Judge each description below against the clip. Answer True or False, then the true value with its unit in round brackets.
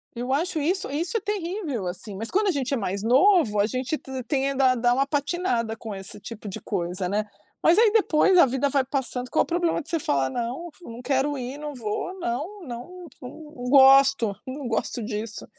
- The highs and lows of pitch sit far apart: True (5.7 semitones)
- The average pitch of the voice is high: True (265 Hz)